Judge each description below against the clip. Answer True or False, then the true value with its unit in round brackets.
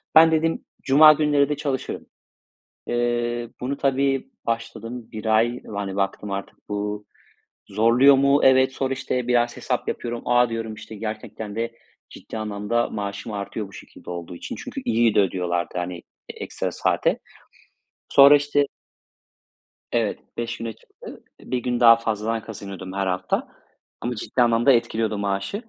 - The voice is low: True (115 Hz)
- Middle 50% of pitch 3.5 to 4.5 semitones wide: True (3.9 semitones)